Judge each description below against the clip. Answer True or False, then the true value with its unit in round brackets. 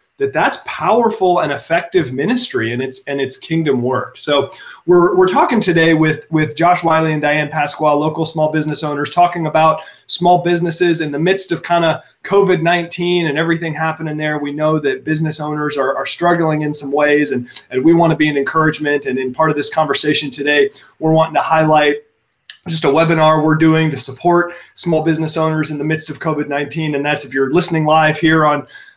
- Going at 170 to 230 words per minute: True (200 wpm)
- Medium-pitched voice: True (155 Hz)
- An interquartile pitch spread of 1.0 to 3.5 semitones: True (2.4 semitones)